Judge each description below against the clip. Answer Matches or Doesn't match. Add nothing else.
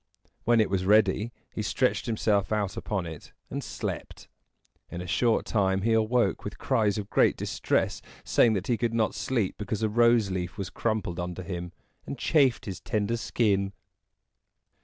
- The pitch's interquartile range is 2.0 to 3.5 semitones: Matches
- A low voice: Matches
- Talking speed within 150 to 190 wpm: Matches